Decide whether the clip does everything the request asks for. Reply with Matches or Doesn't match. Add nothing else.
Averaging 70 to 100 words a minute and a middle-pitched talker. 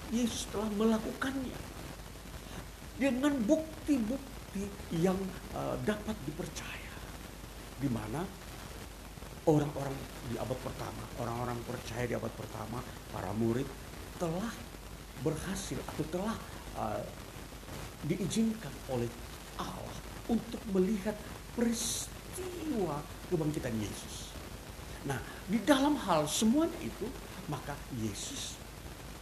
Matches